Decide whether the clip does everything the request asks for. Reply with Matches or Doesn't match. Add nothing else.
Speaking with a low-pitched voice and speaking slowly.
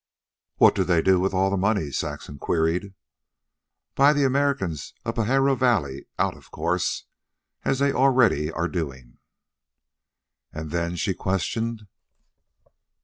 Matches